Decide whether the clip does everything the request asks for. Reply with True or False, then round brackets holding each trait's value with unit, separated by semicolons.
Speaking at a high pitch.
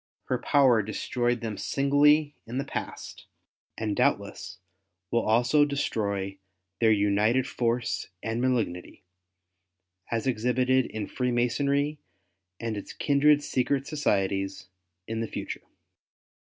False (120 Hz)